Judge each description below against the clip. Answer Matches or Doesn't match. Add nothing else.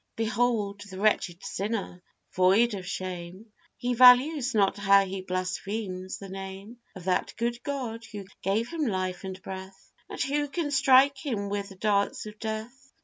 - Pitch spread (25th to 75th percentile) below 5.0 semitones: Matches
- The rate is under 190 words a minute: Matches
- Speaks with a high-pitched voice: Matches